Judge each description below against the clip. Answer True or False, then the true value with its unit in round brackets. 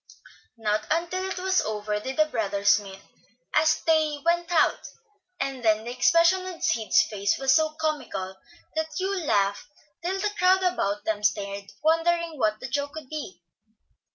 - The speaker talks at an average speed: True (160 wpm)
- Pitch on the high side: True (290 Hz)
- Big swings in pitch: True (8.1 semitones)